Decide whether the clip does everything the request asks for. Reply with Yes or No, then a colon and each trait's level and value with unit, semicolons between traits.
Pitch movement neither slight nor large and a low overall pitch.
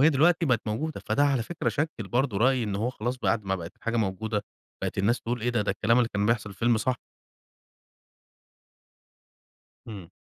Yes: average, 3.7 semitones; low, 115 Hz